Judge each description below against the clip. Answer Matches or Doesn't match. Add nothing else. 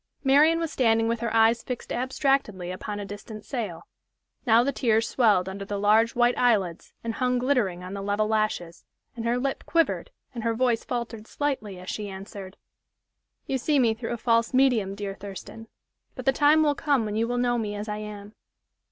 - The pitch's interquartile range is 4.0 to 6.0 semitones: Doesn't match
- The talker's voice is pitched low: Doesn't match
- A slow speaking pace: Doesn't match